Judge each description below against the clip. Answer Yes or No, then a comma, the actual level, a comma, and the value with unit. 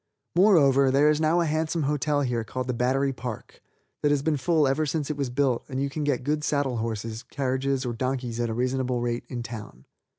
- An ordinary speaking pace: No, fast, 210 wpm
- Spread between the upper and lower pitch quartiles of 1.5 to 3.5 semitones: Yes, average, 3.2 semitones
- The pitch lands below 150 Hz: Yes, low, 135 Hz